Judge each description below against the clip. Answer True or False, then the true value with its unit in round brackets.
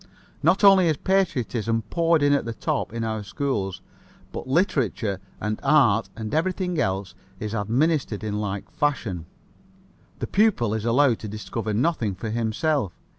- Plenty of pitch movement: True (6.3 semitones)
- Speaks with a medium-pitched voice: False (115 Hz)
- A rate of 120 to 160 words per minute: True (150 wpm)